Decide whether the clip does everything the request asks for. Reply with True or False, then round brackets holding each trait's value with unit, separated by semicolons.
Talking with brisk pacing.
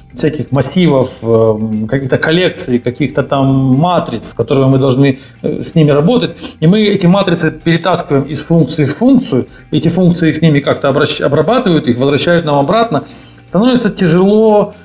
False (135 wpm)